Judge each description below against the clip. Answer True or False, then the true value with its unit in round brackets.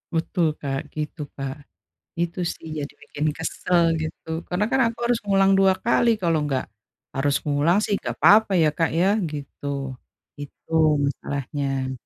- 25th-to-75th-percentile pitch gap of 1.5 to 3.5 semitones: False (5.0 semitones)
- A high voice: False (160 Hz)